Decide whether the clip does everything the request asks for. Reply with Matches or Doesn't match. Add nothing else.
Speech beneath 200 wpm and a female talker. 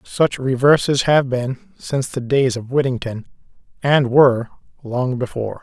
Doesn't match